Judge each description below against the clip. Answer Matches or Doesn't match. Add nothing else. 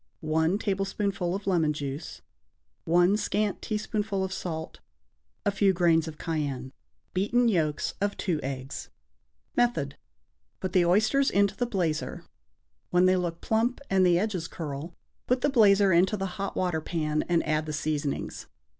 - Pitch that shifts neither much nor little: Matches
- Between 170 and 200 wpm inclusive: Doesn't match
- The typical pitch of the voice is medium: Matches